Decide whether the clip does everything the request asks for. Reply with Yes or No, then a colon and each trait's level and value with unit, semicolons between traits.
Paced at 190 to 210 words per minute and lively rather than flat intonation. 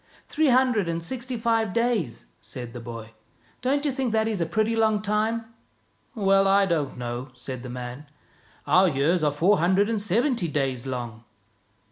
Yes: average, 195 wpm; wide, 9.0 semitones